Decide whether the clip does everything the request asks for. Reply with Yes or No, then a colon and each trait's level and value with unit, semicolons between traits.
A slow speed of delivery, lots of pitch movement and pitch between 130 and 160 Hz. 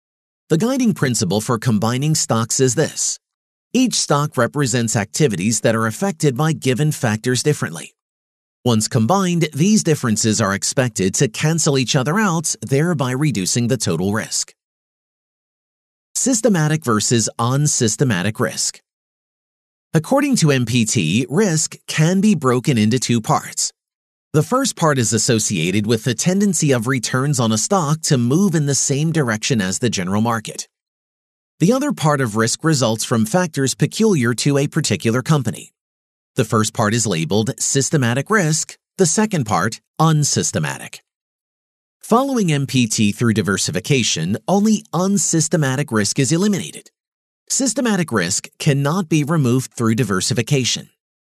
Yes: slow, 130 wpm; wide, 5.9 semitones; medium, 140 Hz